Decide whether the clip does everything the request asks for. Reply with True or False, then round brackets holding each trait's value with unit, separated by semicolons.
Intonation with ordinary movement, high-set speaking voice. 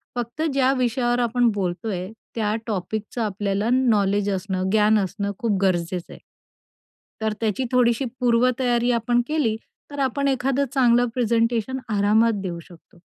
True (3.4 semitones; 230 Hz)